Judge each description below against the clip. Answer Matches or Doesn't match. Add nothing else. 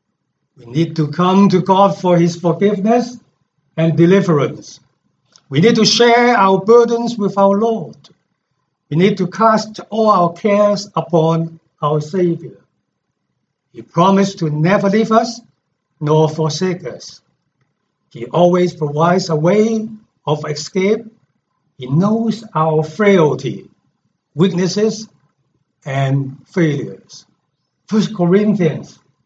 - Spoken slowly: Matches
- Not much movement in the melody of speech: Doesn't match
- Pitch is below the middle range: Doesn't match